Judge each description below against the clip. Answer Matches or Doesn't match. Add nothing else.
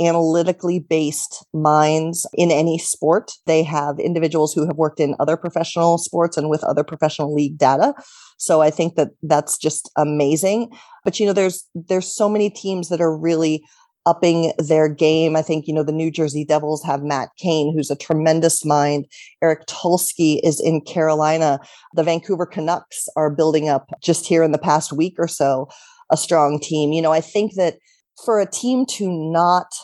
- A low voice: Doesn't match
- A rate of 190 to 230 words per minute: Doesn't match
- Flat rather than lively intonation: Matches